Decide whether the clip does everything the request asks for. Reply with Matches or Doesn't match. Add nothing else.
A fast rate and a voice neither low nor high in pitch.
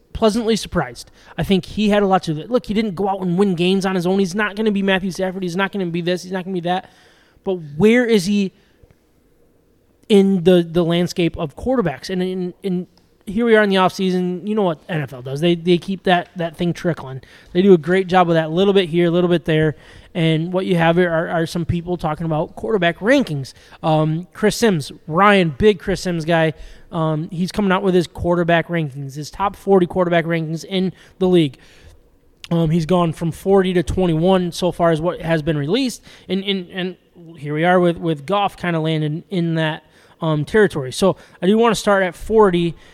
Matches